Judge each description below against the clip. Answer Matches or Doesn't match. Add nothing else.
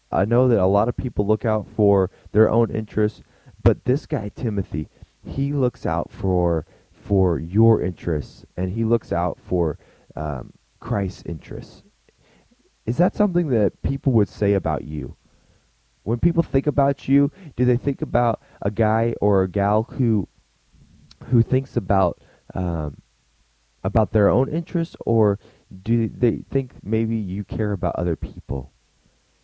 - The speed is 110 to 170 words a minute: Matches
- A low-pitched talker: Matches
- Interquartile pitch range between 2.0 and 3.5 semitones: Doesn't match